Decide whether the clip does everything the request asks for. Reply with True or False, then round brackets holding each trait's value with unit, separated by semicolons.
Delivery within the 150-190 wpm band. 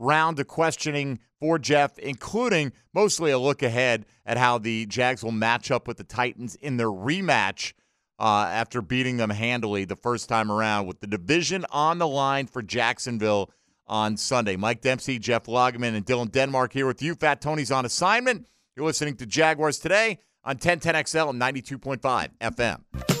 True (170 wpm)